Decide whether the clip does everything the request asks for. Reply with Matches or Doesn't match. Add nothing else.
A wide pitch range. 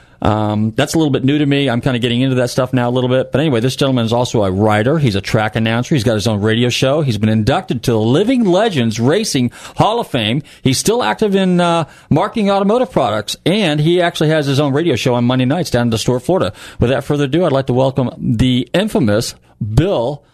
Doesn't match